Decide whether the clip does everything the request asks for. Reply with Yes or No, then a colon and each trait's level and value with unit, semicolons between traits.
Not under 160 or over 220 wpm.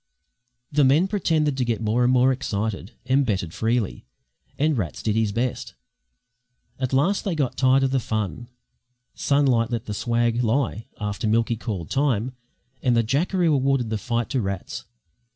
Yes: average, 165 wpm